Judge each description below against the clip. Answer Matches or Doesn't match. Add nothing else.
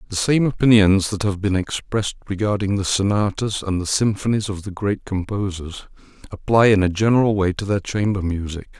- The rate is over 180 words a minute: Doesn't match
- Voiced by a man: Matches